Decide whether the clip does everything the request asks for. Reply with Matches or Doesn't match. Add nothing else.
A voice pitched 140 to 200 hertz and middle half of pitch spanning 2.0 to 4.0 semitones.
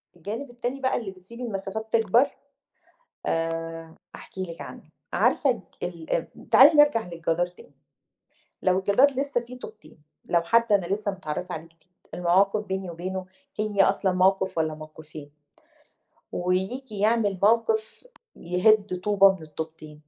Doesn't match